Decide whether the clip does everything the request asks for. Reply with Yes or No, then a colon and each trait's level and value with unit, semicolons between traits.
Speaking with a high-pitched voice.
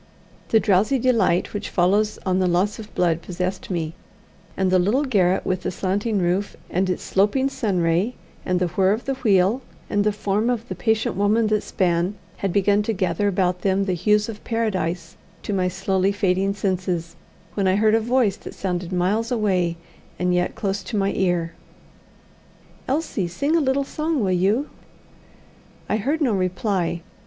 Yes: high, 195 Hz